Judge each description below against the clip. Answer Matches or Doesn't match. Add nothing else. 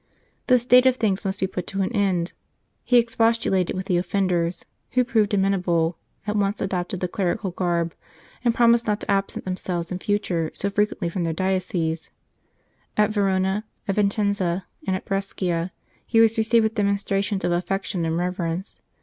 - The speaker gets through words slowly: Doesn't match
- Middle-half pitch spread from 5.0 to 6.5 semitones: Doesn't match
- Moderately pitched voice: Doesn't match